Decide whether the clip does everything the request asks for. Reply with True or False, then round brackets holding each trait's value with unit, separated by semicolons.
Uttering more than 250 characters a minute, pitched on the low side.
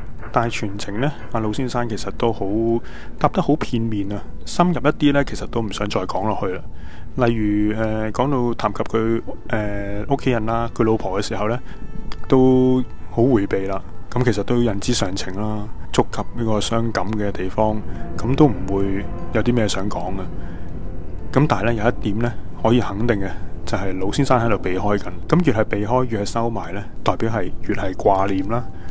True (280 characters per minute; 110 Hz)